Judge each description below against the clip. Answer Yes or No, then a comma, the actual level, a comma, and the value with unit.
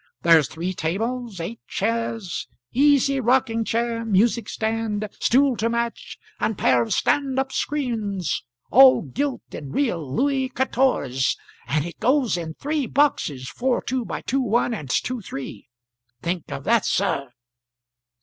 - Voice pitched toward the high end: Yes, high, 230 Hz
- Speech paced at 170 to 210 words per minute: No, average, 140 wpm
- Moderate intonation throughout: No, wide, 7.0 semitones